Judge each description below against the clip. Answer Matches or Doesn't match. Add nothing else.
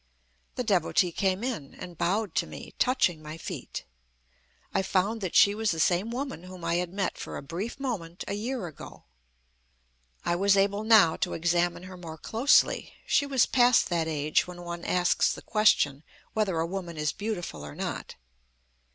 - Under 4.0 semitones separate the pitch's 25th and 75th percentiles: Doesn't match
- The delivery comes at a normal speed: Matches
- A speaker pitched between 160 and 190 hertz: Matches